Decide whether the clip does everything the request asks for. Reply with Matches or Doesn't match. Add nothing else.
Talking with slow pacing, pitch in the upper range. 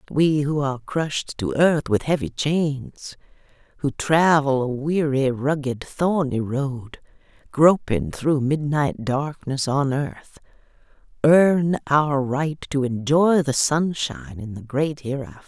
Doesn't match